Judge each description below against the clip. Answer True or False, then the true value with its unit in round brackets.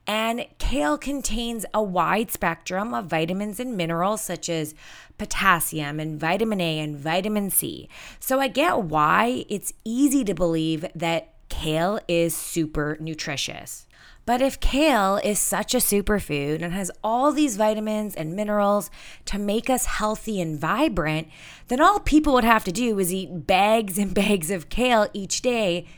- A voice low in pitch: False (205 Hz)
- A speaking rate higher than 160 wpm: False (155 wpm)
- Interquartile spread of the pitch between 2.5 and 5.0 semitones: False (5.4 semitones)